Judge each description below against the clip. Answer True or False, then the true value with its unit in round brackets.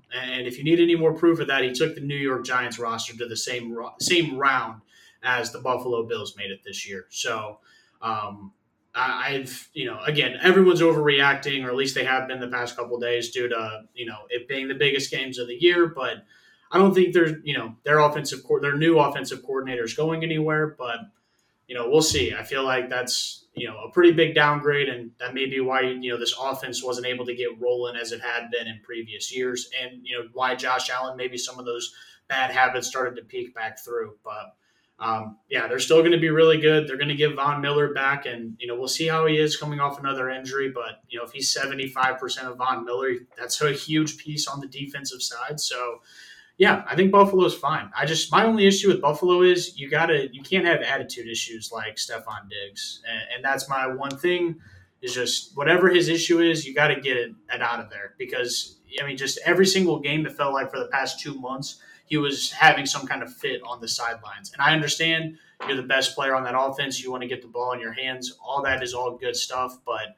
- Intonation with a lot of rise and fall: False (3.8 semitones)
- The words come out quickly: True (230 wpm)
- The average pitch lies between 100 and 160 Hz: True (135 Hz)